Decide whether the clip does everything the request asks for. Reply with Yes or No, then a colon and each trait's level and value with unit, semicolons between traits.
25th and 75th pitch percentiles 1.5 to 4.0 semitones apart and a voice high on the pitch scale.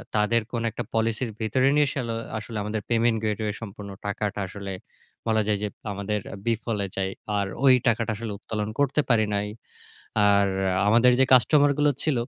No: narrow, 2.4 semitones; low, 110 Hz